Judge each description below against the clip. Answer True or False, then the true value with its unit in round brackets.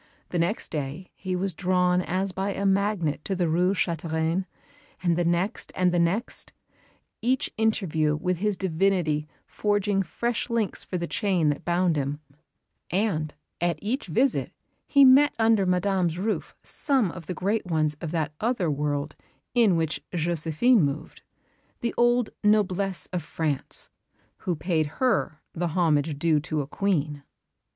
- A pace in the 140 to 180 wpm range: True (150 wpm)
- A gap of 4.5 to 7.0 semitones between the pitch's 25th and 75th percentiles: False (4.1 semitones)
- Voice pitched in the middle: True (180 Hz)